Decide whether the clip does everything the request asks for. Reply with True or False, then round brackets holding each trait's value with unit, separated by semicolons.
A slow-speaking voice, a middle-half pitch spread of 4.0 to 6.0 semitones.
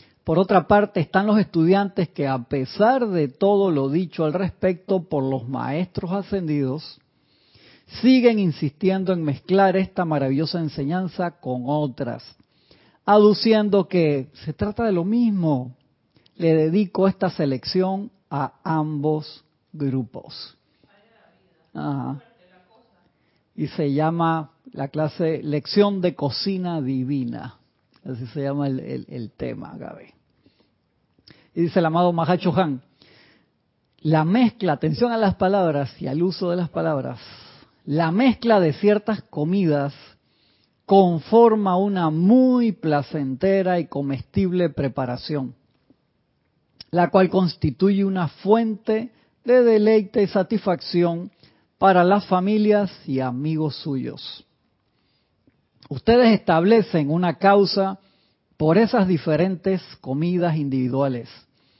True (110 wpm; 5.1 semitones)